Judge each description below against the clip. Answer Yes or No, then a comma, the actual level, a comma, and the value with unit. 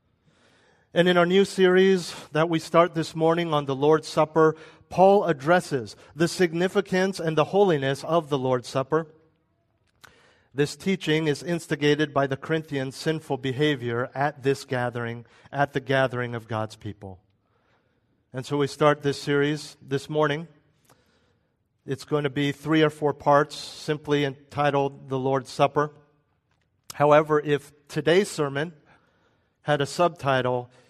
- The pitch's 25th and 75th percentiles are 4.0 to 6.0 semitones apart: No, average, 2.9 semitones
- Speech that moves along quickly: No, average, 140 wpm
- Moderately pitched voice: Yes, medium, 145 Hz